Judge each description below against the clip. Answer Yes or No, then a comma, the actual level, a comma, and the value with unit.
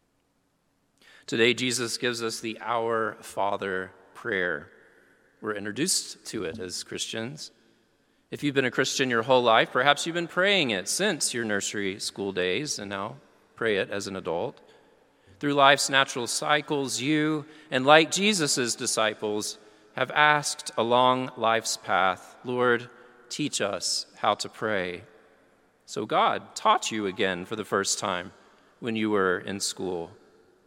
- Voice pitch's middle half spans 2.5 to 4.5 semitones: No, average, 5.0 semitones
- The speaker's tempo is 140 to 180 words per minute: Yes, average, 145 wpm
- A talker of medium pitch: No, low, 120 Hz